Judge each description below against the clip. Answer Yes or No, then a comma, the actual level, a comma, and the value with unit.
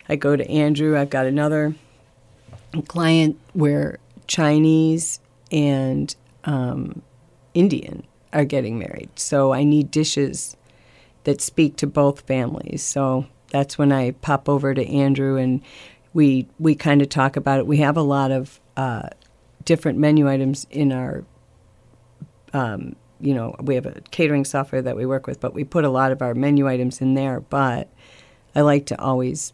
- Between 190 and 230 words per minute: No, average, 160 wpm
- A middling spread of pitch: No, narrow, 2.1 semitones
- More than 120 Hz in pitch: Yes, medium, 140 Hz